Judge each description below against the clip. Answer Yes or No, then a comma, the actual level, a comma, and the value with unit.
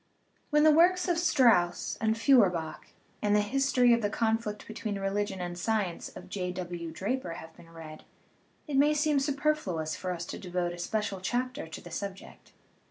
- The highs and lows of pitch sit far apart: Yes, wide, 6.9 semitones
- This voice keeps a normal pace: Yes, average, 175 wpm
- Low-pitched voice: No, high, 205 Hz